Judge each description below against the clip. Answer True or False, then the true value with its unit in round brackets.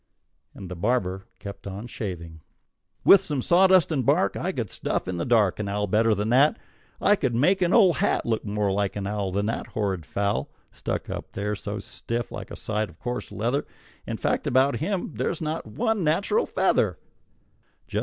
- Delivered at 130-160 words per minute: False (190 wpm)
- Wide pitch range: True (7.1 semitones)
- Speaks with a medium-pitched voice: False (110 Hz)